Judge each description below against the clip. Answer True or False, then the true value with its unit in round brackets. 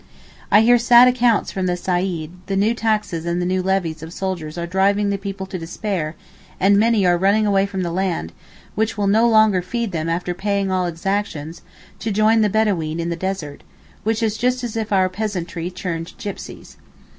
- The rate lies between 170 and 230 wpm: True (195 wpm)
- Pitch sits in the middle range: False (195 Hz)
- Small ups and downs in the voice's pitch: False (3.5 semitones)